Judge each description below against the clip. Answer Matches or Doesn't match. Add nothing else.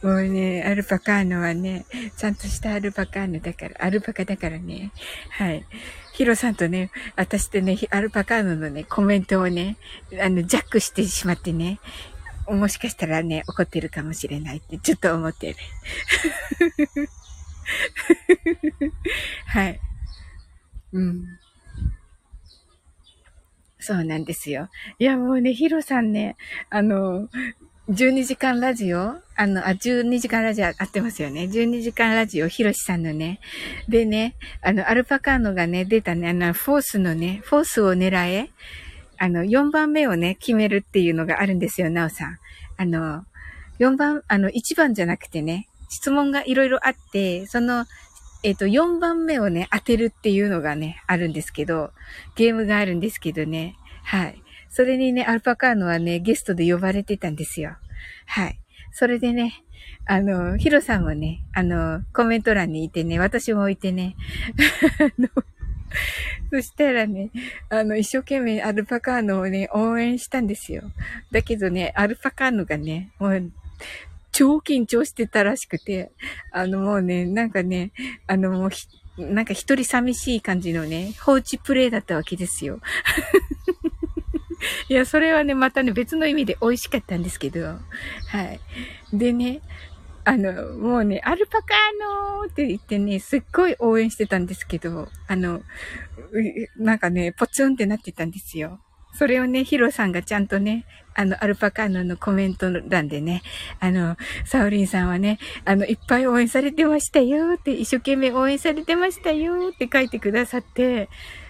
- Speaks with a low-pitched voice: Doesn't match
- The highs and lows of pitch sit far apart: Matches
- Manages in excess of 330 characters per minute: Doesn't match